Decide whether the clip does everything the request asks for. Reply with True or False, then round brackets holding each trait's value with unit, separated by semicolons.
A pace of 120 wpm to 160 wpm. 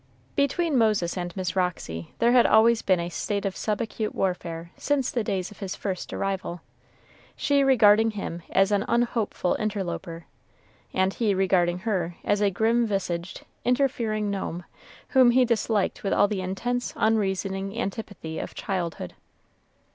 True (150 wpm)